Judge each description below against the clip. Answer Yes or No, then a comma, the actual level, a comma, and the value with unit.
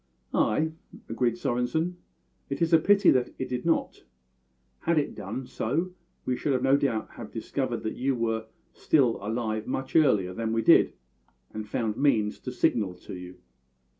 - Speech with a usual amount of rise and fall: Yes, average, 4.5 semitones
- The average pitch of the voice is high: No, low, 125 Hz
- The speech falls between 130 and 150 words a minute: No, average, 165 wpm